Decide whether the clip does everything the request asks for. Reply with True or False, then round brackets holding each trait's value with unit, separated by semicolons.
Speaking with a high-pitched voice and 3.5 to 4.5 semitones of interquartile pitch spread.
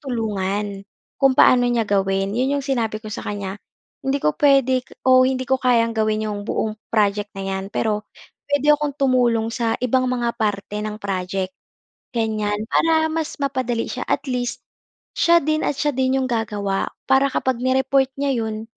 True (240 Hz; 4.1 semitones)